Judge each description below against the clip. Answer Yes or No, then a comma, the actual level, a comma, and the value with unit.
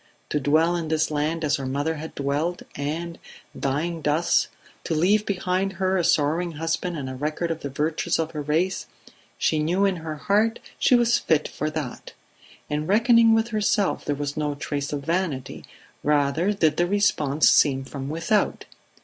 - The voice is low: No, medium, 160 Hz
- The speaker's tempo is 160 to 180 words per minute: Yes, average, 175 wpm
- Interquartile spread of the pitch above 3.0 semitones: Yes, average, 3.7 semitones